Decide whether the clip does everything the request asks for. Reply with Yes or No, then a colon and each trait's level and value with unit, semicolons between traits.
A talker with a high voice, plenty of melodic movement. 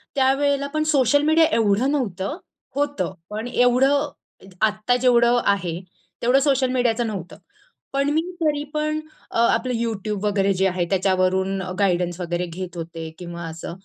Yes: high, 230 Hz; wide, 6.6 semitones